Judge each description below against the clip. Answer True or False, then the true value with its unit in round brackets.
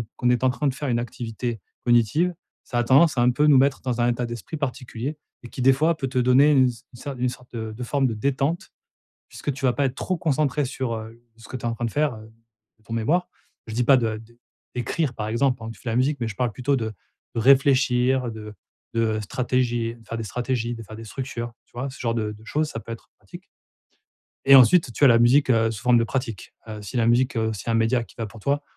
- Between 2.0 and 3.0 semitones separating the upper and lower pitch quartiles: True (2.7 semitones)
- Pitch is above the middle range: False (125 Hz)